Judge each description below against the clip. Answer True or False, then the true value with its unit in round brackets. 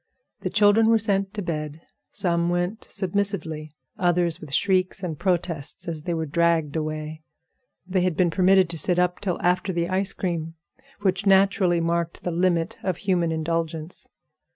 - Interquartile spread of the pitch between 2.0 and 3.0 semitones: True (2.5 semitones)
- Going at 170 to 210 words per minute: False (160 wpm)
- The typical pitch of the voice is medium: True (175 Hz)